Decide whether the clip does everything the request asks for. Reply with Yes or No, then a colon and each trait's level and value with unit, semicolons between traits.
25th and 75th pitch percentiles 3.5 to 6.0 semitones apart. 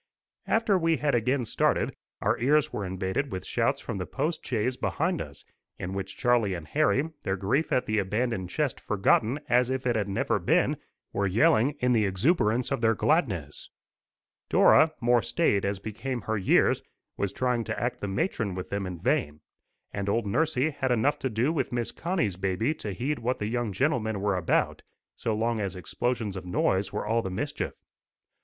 Yes: average, 5.1 semitones